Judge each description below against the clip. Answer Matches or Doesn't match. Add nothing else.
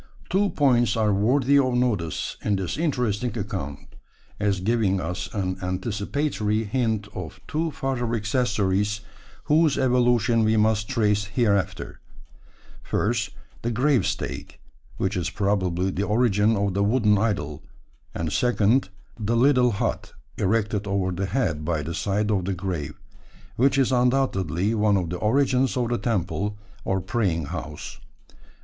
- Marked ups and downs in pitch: Doesn't match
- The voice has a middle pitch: Doesn't match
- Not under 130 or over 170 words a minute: Matches